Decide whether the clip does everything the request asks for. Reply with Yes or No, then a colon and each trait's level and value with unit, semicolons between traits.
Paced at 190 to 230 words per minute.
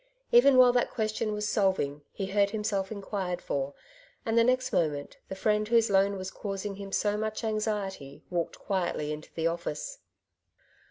No: average, 165 wpm